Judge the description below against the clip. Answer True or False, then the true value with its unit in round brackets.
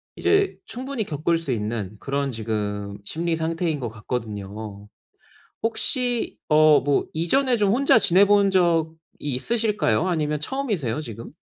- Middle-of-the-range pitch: True (155 Hz)